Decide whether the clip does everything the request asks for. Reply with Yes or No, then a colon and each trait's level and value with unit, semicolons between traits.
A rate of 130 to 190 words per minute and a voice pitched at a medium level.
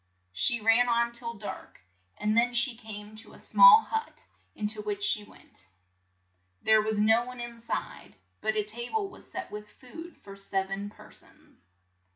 No: average, 185 wpm; high, 220 Hz